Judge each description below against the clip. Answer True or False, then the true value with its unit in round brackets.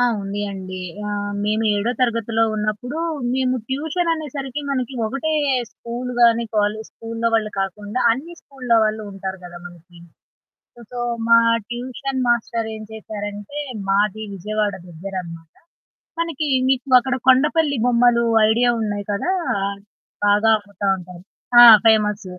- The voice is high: True (220 Hz)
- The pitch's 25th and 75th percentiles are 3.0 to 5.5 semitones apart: True (3.7 semitones)